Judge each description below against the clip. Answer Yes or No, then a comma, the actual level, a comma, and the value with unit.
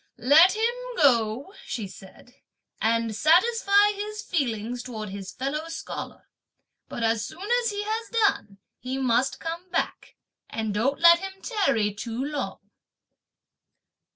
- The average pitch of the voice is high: Yes, very high, 275 Hz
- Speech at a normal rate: No, slow, 130 wpm